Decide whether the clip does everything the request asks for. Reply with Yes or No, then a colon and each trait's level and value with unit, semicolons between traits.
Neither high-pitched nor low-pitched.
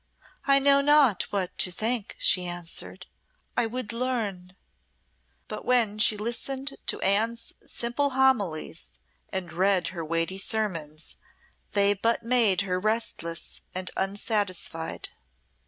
No: high, 205 Hz